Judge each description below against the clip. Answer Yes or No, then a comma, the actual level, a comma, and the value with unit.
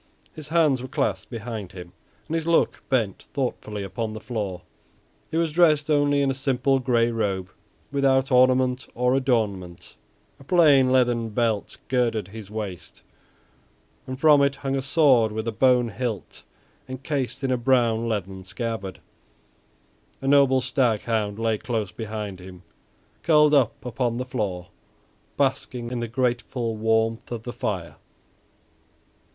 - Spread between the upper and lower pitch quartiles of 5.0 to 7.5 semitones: No, average, 3.7 semitones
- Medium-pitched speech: No, low, 120 Hz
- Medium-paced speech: Yes, average, 145 wpm